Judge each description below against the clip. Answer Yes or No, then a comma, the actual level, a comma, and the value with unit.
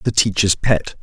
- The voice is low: Yes, low, 100 Hz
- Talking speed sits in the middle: Yes, average, 175 wpm